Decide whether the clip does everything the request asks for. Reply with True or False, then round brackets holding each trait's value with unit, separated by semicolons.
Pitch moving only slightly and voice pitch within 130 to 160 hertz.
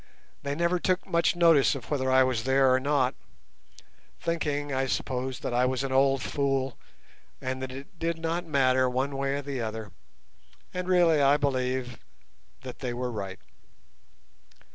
True (2.2 semitones; 135 Hz)